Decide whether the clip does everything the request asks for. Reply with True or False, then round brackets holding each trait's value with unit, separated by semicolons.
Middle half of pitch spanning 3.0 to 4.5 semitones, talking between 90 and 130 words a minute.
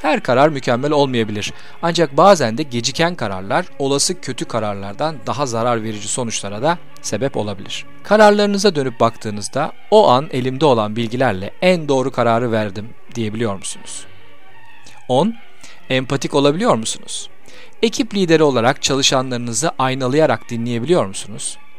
False (5.0 semitones; 120 wpm)